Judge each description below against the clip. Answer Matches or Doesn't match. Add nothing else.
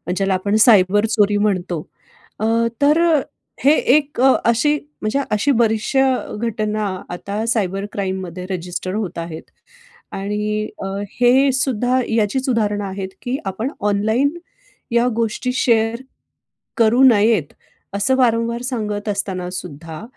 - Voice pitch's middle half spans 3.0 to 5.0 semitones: Matches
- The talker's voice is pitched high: Matches